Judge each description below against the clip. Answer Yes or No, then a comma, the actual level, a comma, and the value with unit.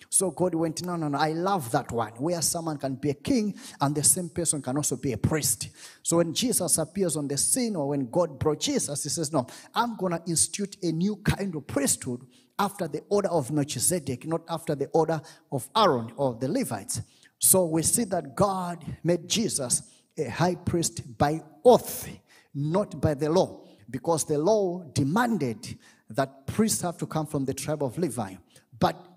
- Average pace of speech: Yes, average, 190 wpm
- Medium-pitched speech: Yes, medium, 160 Hz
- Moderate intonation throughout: Yes, average, 4.0 semitones